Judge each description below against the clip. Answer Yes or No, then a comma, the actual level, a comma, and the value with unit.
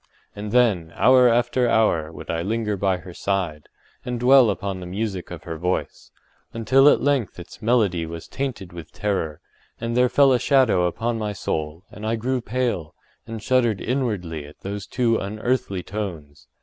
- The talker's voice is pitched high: No, low, 105 Hz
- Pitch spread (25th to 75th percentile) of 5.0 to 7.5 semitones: Yes, wide, 5.5 semitones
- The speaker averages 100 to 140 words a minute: No, average, 175 wpm